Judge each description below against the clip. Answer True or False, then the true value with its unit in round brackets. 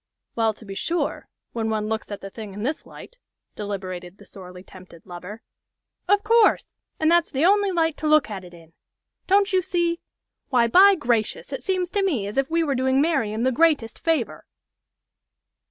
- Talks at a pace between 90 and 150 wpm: False (185 wpm)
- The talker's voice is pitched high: True (260 Hz)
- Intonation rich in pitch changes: True (8.6 semitones)